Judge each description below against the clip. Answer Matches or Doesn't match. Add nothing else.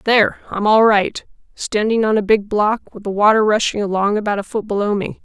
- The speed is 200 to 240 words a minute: Matches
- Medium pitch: Doesn't match